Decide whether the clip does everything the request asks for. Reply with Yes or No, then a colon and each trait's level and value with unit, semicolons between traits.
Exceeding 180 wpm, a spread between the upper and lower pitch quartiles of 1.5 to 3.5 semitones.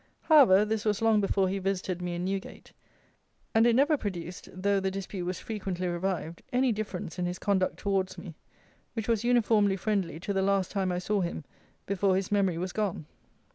Yes: average, 190 wpm; narrow, 2.5 semitones